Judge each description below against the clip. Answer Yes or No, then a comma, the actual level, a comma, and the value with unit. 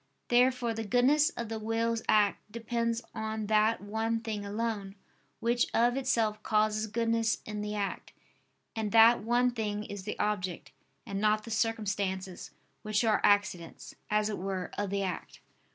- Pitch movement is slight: Yes, narrow, 1.9 semitones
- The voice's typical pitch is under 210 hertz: No, high, 215 Hz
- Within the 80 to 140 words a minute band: No, average, 155 wpm